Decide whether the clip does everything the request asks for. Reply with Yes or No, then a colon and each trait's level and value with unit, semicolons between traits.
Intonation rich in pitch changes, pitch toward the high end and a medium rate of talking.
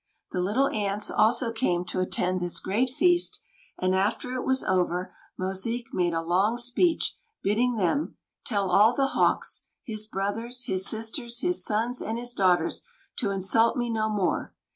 No: average, 4.3 semitones; high, 215 Hz; average, 165 wpm